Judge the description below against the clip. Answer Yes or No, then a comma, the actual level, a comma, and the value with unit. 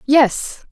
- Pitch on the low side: No, very high, 275 Hz